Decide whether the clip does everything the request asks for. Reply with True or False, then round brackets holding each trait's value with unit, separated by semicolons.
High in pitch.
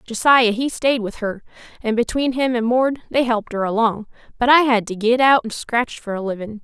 True (235 Hz)